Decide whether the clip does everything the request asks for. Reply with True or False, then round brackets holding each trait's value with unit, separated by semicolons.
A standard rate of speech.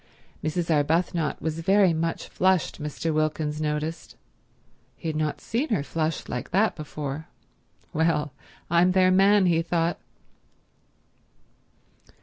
False (120 wpm)